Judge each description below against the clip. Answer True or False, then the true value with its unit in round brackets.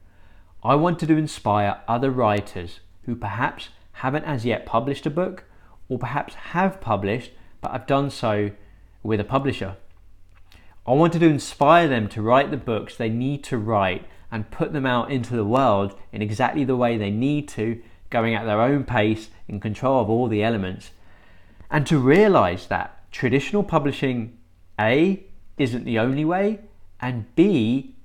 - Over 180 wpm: False (165 wpm)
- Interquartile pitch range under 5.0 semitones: False (5.3 semitones)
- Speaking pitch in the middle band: False (115 Hz)